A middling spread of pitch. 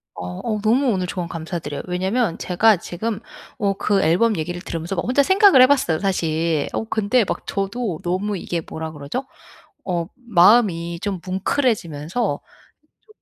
Yes: average, 5.0 semitones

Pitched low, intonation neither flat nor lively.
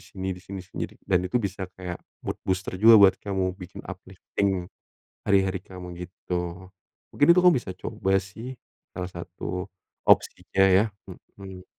No: very low, 95 Hz; narrow, 1.3 semitones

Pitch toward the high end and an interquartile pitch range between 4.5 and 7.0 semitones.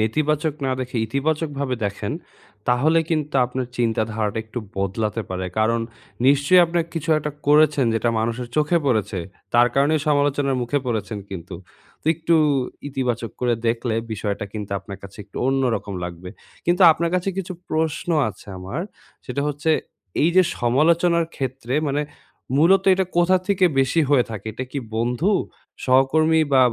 No: low, 135 Hz; wide, 5.5 semitones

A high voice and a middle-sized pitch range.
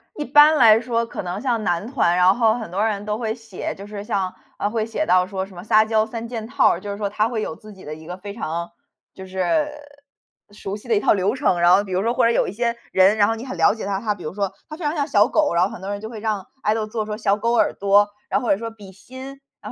Yes: high, 210 Hz; average, 3.1 semitones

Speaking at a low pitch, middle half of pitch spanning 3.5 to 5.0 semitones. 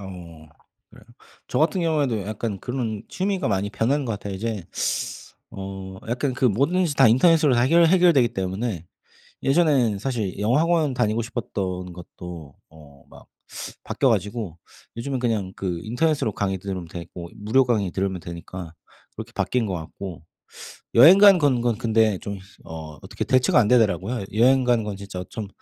No: low, 110 Hz; wide, 5.5 semitones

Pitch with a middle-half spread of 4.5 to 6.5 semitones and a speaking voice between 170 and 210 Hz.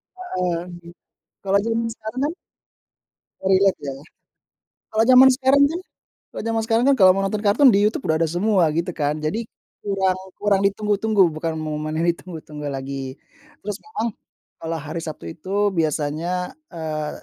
Yes: wide, 5.6 semitones; high, 190 Hz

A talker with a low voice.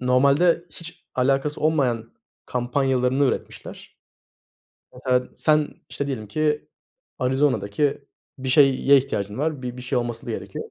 Yes: low, 130 Hz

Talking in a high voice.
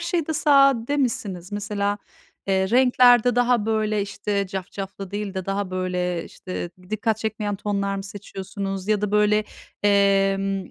Yes: high, 205 Hz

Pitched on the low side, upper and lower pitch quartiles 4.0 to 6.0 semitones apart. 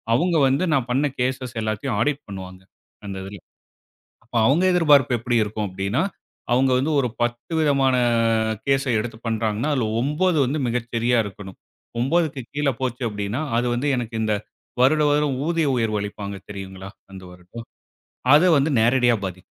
Yes: low, 120 Hz; average, 4.7 semitones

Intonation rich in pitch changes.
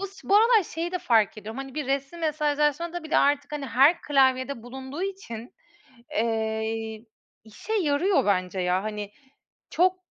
Yes: wide, 7.0 semitones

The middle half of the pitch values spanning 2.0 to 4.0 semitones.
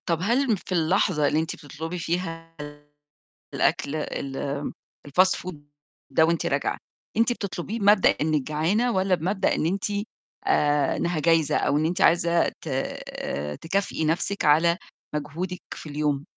Yes: average, 3.6 semitones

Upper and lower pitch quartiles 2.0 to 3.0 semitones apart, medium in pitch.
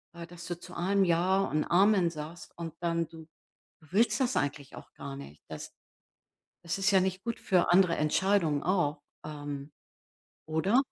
No: average, 3.7 semitones; medium, 170 Hz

